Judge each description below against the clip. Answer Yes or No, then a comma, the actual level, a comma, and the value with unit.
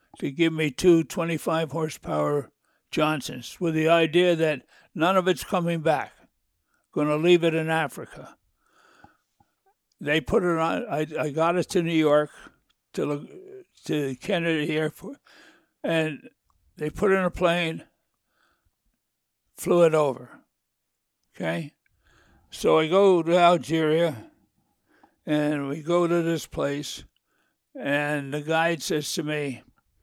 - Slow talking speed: Yes, slow, 130 wpm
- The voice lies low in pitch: No, medium, 160 Hz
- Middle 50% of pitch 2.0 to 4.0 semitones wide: Yes, narrow, 2.4 semitones